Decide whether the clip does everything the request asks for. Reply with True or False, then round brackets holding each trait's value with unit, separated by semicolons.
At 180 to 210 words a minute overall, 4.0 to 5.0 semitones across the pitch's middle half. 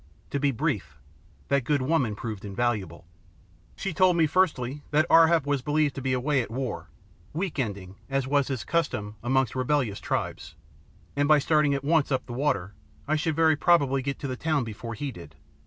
True (190 wpm; 4.4 semitones)